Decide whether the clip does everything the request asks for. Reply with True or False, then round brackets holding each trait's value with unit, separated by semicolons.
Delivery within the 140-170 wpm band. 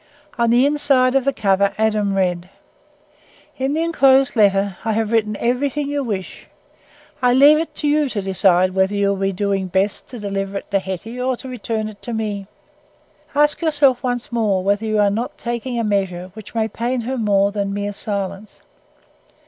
False (190 wpm)